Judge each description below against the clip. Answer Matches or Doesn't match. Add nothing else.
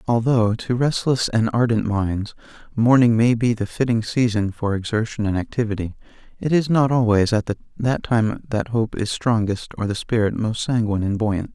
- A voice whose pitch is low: Matches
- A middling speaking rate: Matches